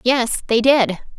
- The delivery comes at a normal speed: Yes, average, 150 wpm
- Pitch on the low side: No, high, 240 Hz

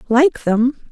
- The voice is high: Yes, very high, 255 Hz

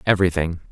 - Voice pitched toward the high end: No, very low, 85 Hz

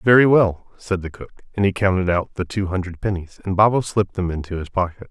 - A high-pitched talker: No, very low, 95 Hz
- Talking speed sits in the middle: No, fast, 235 wpm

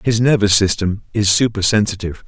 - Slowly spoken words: Yes, slow, 130 wpm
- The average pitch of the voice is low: Yes, low, 105 Hz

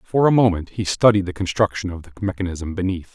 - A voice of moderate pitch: No, very low, 95 Hz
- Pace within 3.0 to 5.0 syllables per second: No, 6.1 syllables/s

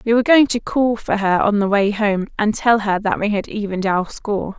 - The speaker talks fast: Yes, fast, 260 wpm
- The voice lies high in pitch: Yes, high, 210 Hz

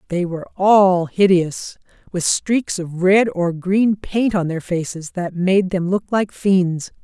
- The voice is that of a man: No, female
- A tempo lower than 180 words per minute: Yes, average, 160 wpm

